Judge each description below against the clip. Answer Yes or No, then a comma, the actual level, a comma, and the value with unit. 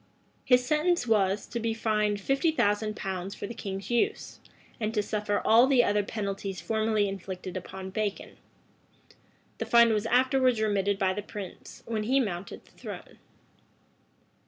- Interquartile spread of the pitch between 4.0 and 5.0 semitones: No, average, 3.0 semitones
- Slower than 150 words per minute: No, average, 155 wpm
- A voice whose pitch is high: Yes, high, 215 Hz